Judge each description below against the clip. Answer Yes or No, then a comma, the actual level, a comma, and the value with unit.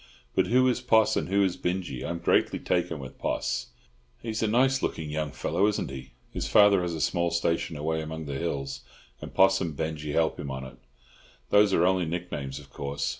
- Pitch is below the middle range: Yes, very low, 85 Hz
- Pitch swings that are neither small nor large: Yes, average, 5.0 semitones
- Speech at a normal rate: No, fast, 210 wpm